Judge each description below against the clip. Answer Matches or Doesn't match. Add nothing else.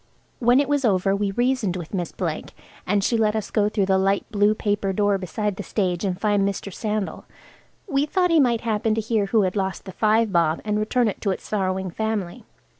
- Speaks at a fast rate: Matches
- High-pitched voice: Matches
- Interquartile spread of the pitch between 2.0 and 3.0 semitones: Matches